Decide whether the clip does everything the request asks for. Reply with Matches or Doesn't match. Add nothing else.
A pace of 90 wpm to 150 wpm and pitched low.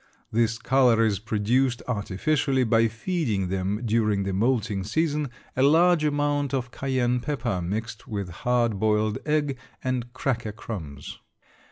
Matches